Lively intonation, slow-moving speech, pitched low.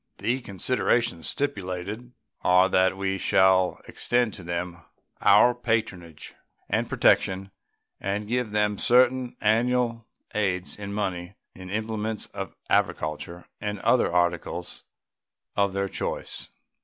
No: average, 3.7 semitones; slow, 115 wpm; low, 100 Hz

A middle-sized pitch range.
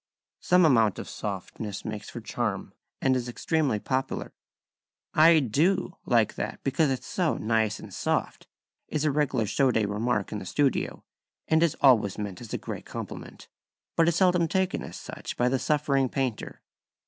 No: wide, 5.9 semitones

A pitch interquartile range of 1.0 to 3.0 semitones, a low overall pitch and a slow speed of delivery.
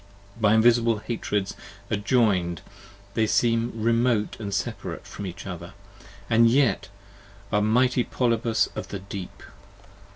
Yes: narrow, 2.6 semitones; low, 110 Hz; slow, 125 wpm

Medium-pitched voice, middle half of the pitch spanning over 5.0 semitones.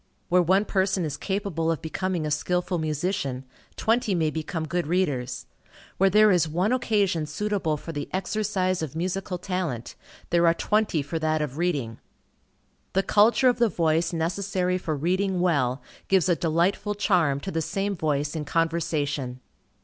No: medium, 170 Hz; average, 3.6 semitones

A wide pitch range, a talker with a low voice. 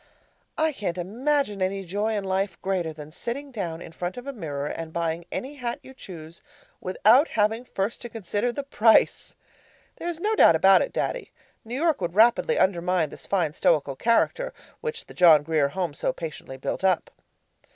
No: wide, 6.5 semitones; high, 195 Hz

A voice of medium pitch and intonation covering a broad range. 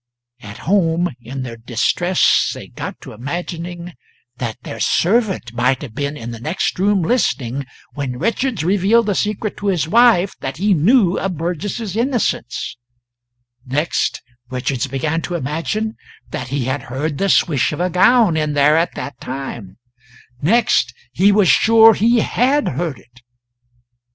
Yes: medium, 165 Hz; wide, 7.3 semitones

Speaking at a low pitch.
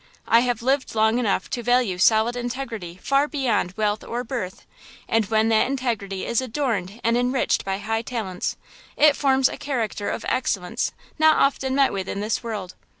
No: high, 230 Hz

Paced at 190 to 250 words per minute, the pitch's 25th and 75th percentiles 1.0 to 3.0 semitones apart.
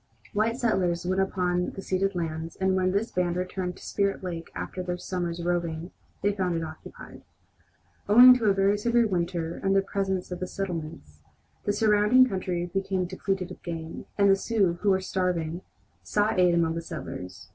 No: average, 180 wpm; narrow, 2.4 semitones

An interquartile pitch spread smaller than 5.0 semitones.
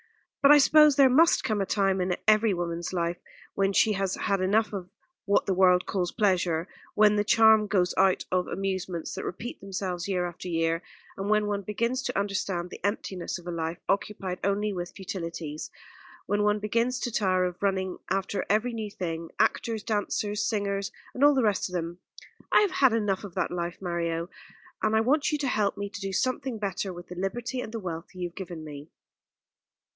Yes: average, 3.1 semitones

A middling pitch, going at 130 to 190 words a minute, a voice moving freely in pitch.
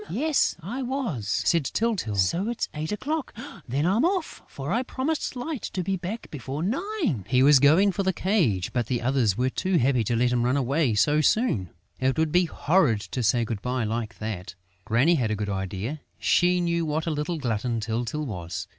No: medium, 145 Hz; average, 200 wpm; wide, 8.4 semitones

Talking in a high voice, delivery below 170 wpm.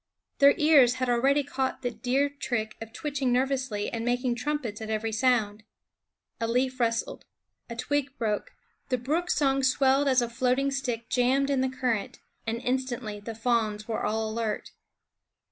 Yes: very high, 250 Hz; average, 160 wpm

